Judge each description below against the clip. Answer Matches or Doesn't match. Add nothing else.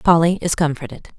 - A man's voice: Doesn't match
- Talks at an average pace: Matches